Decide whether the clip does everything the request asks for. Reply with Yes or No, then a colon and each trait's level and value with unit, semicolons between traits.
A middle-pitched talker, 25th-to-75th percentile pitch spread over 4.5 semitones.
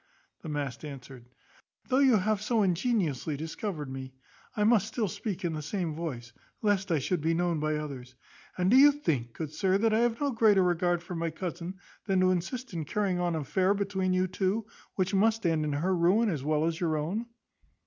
Yes: medium, 180 Hz; average, 4.9 semitones